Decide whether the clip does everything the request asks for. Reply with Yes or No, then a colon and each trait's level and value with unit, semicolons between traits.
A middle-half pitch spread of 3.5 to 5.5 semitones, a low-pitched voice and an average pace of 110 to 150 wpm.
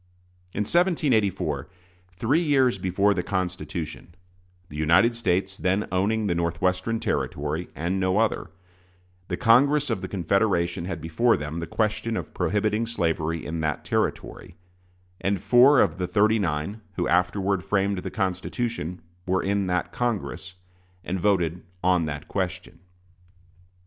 Yes: average, 3.9 semitones; very low, 95 Hz; slow, 135 wpm